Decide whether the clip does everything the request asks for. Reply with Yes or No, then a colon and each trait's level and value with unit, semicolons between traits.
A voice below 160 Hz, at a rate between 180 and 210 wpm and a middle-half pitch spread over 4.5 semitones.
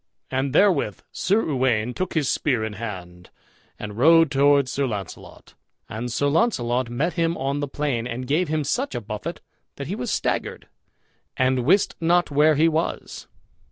No: medium, 140 Hz; average, 165 wpm; average, 5.1 semitones